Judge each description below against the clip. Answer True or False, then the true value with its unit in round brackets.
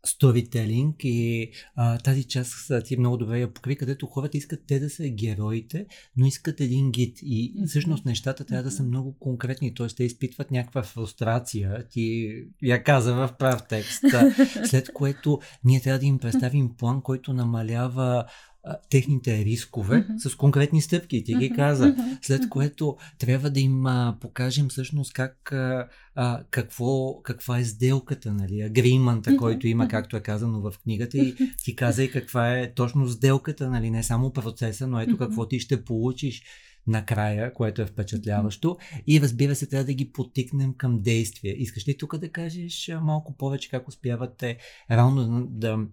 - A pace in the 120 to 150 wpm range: False (160 wpm)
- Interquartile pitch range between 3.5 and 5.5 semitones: False (2.8 semitones)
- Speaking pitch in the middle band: False (130 Hz)